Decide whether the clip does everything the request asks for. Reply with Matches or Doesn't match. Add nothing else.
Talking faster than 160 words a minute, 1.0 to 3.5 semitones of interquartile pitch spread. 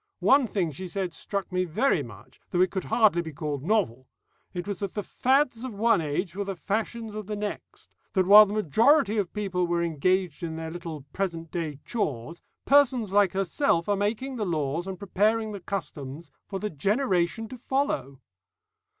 Doesn't match